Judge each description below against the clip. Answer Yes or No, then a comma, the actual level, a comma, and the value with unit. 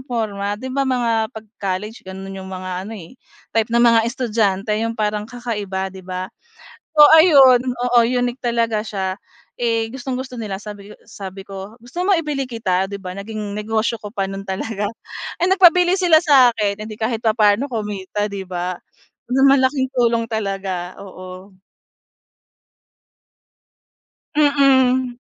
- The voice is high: Yes, high, 220 Hz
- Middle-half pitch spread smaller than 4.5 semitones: Yes, average, 4.1 semitones